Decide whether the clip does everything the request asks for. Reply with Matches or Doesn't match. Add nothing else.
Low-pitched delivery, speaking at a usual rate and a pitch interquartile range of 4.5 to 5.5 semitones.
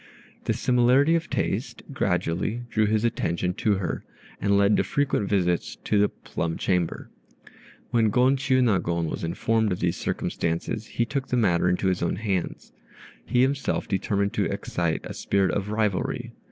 Matches